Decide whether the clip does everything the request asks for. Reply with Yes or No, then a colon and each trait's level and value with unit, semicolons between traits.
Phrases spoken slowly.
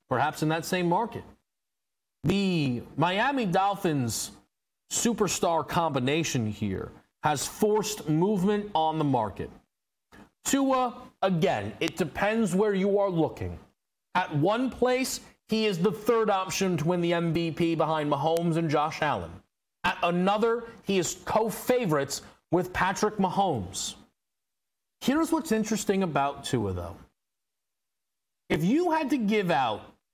Yes: slow, 125 wpm